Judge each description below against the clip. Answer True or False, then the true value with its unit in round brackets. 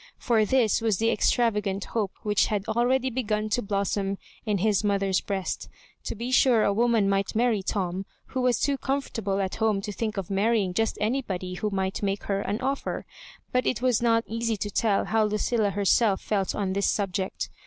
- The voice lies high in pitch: True (210 Hz)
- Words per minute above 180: True (190 wpm)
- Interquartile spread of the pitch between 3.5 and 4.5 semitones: False (2.8 semitones)